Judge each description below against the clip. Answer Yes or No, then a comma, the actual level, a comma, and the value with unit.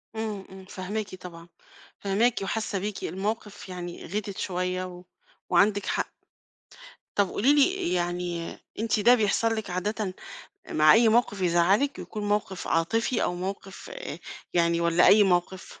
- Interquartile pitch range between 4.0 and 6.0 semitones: No, average, 3.3 semitones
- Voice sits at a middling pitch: No, high, 195 Hz